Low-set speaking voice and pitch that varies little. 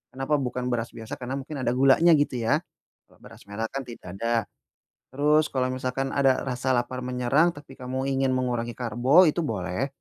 Yes: low, 130 Hz; narrow, 2.1 semitones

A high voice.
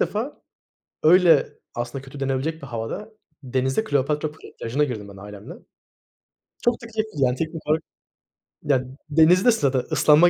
No: medium, 145 Hz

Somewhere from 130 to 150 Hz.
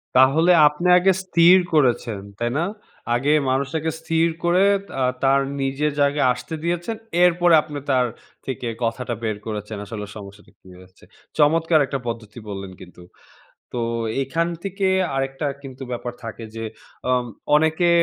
Yes: low, 135 Hz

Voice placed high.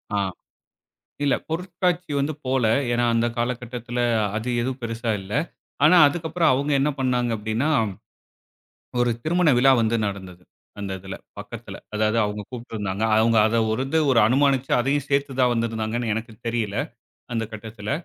No: low, 120 Hz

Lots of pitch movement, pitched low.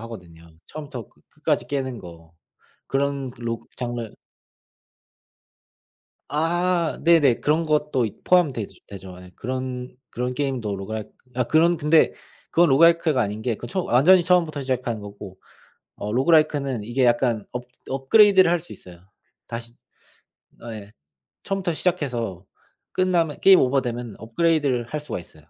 Yes: wide, 5.7 semitones; low, 130 Hz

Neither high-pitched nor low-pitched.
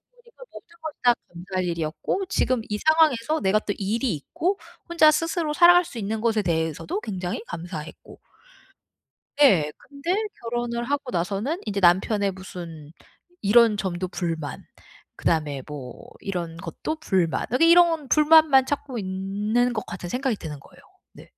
No: high, 210 Hz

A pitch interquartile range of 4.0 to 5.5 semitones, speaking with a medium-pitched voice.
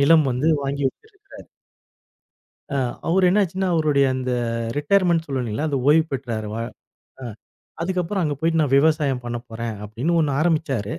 Yes: average, 4.4 semitones; medium, 150 Hz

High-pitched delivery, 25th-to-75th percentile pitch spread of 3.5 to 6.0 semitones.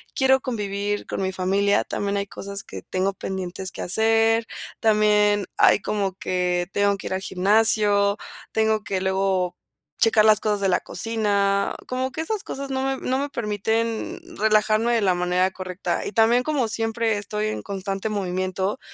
No: high, 205 Hz; narrow, 2.6 semitones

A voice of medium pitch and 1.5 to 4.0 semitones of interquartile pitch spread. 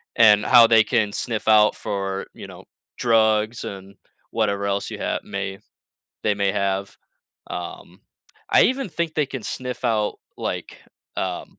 No: low, 105 Hz; average, 2.8 semitones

